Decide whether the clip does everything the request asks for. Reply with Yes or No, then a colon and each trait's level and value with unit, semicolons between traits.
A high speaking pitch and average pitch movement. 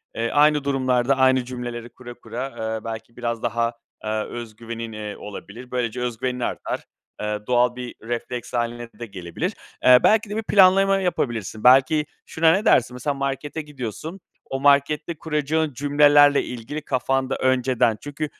No: low, 125 Hz; average, 3.7 semitones